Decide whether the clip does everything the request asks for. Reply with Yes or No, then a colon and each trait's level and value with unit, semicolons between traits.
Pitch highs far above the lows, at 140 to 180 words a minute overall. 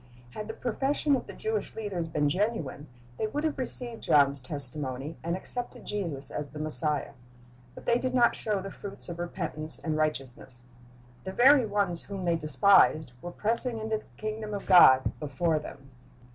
Yes: wide, 6.6 semitones; average, 175 wpm